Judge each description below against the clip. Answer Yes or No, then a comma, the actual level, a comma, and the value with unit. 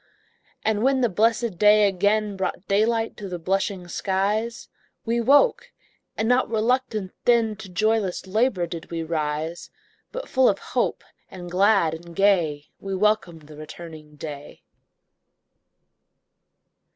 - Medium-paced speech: No, slow, 130 wpm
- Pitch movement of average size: Yes, average, 4.4 semitones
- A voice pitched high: Yes, high, 200 Hz